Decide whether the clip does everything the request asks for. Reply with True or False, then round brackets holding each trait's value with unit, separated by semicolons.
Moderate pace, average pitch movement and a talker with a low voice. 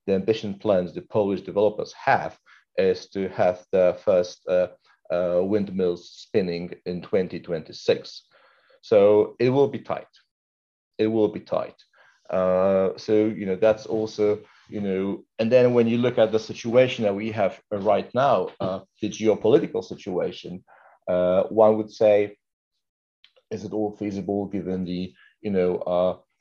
True (150 wpm; 4.5 semitones; 105 Hz)